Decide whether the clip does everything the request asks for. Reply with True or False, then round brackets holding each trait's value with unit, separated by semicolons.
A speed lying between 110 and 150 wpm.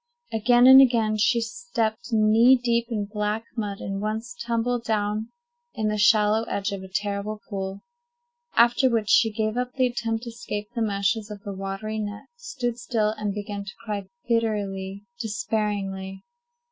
False (160 wpm)